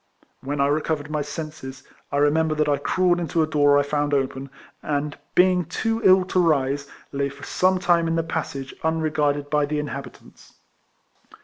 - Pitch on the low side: No, medium, 150 Hz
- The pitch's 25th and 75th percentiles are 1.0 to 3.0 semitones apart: Yes, narrow, 2.4 semitones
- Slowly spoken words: No, average, 175 wpm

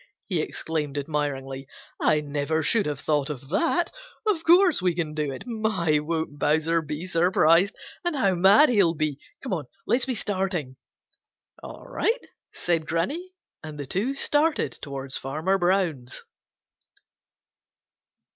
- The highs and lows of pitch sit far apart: Yes, wide, 5.8 semitones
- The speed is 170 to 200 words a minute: No, slow, 135 wpm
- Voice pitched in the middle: Yes, medium, 165 Hz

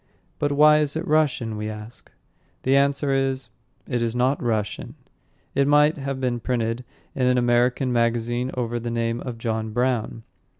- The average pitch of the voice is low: Yes, low, 125 Hz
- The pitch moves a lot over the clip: No, average, 2.8 semitones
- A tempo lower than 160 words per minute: No, average, 165 wpm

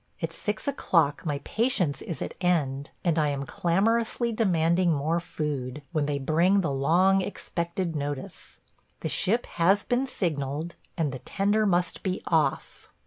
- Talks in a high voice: No, medium, 170 Hz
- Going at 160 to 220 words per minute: No, average, 150 wpm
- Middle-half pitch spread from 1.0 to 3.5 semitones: No, average, 4.8 semitones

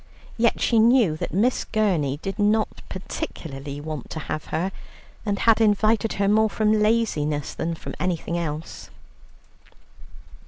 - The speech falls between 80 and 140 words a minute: Yes, slow, 135 wpm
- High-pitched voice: Yes, high, 195 Hz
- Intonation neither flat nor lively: No, wide, 5.7 semitones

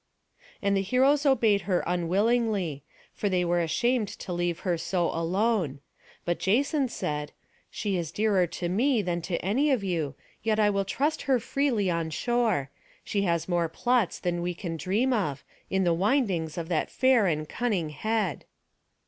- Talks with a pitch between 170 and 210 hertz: Yes, high, 190 Hz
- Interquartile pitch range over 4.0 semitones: Yes, average, 4.9 semitones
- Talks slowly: No, average, 170 wpm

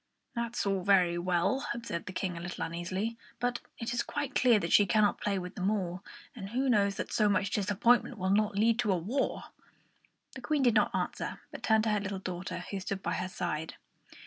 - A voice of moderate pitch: No, high, 200 Hz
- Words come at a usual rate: No, fast, 215 wpm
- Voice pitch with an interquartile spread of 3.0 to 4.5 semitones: Yes, average, 3.9 semitones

